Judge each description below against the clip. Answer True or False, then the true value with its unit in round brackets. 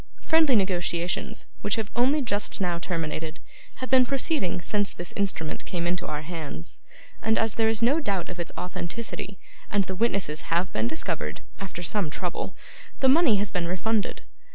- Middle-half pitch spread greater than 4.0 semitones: True (4.6 semitones)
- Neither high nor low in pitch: False (195 Hz)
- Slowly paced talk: False (170 wpm)